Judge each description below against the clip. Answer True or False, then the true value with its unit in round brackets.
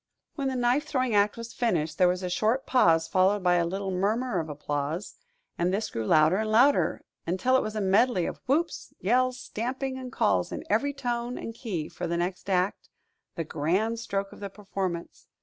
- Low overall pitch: False (200 Hz)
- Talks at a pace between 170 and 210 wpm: True (200 wpm)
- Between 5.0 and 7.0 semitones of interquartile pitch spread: True (5.6 semitones)